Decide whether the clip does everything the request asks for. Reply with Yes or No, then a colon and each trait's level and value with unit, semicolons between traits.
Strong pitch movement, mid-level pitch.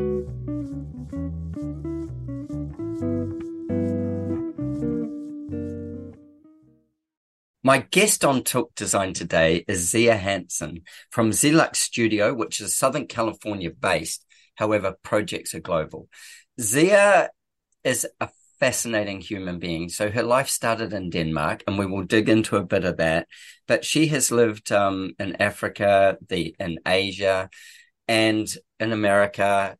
No: wide, 6.4 semitones; low, 105 Hz